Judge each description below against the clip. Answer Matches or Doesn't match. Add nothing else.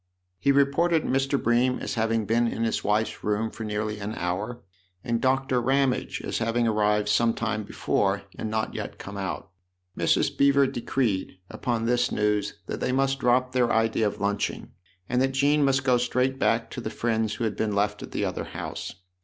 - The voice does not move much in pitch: Doesn't match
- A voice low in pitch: Matches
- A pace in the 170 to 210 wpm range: Matches